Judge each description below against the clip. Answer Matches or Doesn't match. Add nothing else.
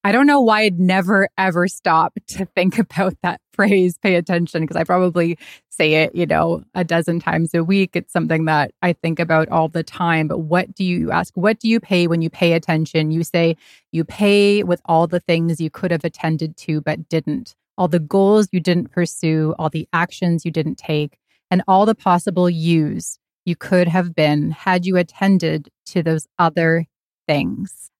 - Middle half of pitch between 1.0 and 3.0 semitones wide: Matches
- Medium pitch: Matches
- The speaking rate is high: Doesn't match